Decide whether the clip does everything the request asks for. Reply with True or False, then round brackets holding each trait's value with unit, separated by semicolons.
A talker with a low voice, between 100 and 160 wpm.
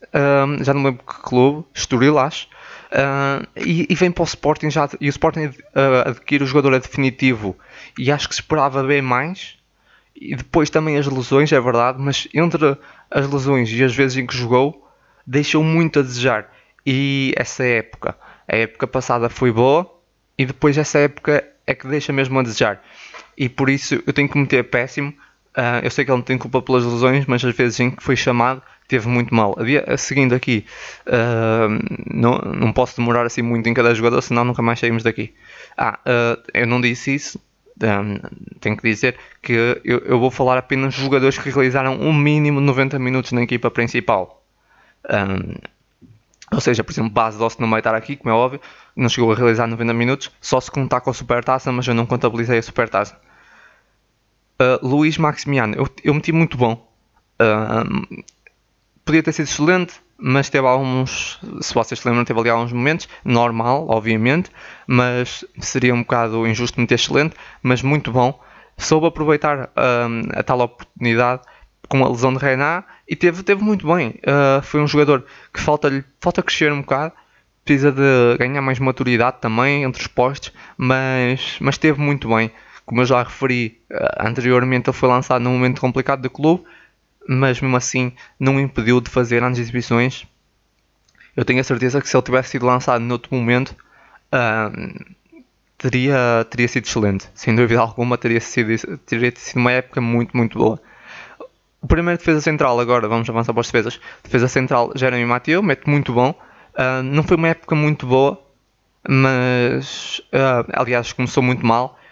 False (130 Hz; 180 wpm)